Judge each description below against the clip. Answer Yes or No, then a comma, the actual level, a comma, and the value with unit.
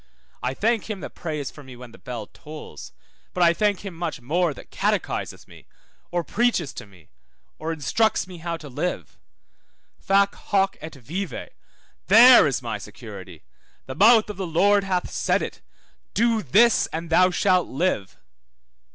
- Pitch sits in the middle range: Yes, medium, 175 Hz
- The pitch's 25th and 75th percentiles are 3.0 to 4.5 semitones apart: No, average, 5.2 semitones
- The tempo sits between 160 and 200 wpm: Yes, average, 165 wpm